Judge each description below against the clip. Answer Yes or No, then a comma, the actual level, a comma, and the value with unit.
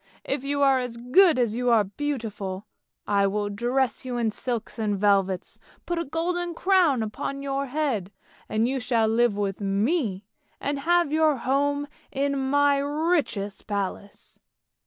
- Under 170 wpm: Yes, average, 155 wpm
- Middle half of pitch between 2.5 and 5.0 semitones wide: No, wide, 5.5 semitones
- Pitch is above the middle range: Yes, very high, 250 Hz